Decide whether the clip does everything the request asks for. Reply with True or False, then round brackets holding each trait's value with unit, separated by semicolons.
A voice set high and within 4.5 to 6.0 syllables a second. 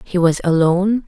False (180 Hz; 5.3 syllables/s)